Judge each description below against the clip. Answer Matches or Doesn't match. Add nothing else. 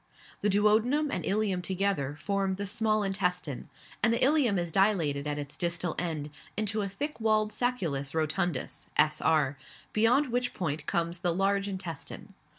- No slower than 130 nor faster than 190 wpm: Matches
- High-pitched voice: Matches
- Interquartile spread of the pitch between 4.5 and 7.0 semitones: Matches